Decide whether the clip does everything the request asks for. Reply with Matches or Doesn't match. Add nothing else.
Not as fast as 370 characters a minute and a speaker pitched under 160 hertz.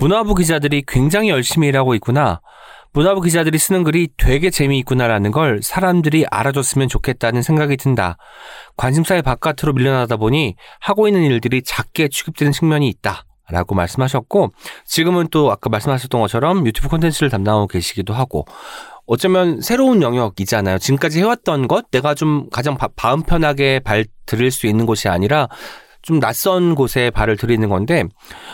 Doesn't match